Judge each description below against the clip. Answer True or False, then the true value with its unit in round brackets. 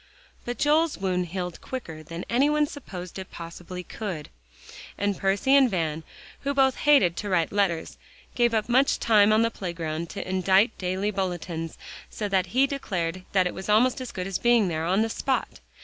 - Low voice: False (195 Hz)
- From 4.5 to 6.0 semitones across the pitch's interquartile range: True (5.2 semitones)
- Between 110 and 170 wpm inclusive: False (185 wpm)